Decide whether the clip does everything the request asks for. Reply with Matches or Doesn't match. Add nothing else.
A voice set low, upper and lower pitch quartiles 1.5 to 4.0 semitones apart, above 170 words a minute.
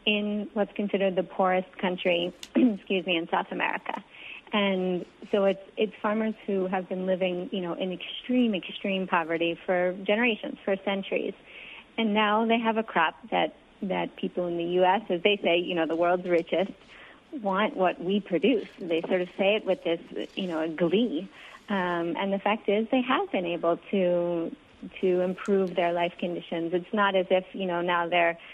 Doesn't match